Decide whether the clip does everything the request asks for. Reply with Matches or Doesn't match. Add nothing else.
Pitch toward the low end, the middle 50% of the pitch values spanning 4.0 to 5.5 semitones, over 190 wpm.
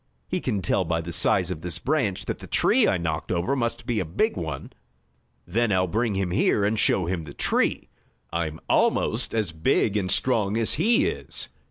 Matches